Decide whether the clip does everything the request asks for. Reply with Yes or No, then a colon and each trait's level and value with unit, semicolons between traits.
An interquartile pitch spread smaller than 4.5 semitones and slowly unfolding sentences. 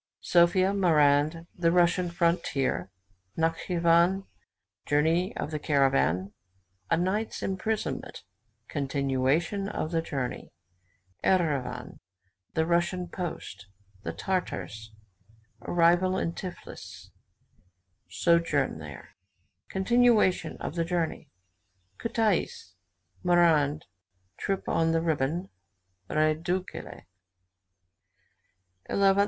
Yes: average, 3.7 semitones; slow, 80 wpm